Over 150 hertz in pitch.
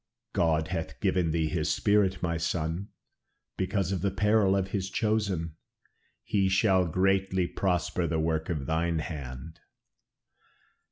No: very low, 90 Hz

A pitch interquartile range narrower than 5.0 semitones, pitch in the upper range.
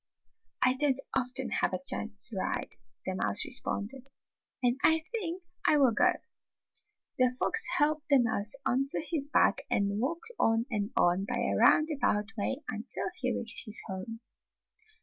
No: wide, 5.6 semitones; very high, 250 Hz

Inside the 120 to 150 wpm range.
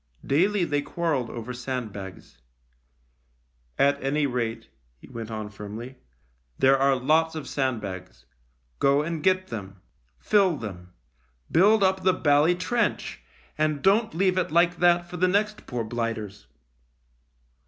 Yes: average, 140 wpm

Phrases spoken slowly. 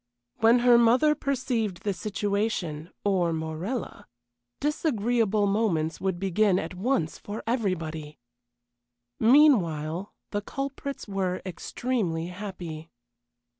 Yes: slow, 95 wpm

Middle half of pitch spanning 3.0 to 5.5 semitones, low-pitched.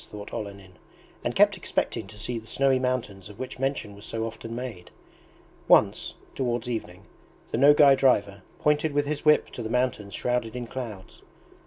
Yes: average, 4.0 semitones; low, 120 Hz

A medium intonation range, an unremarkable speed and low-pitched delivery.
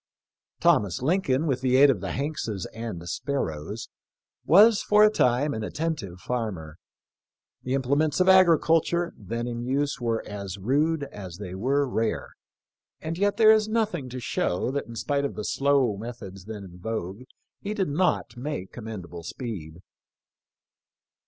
No: wide, 6.8 semitones; average, 150 wpm; low, 125 Hz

